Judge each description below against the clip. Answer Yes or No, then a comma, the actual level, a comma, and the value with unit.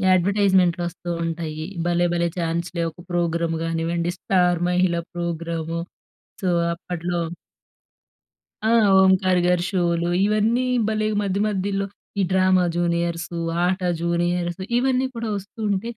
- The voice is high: No, medium, 175 Hz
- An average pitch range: No, narrow, 2.0 semitones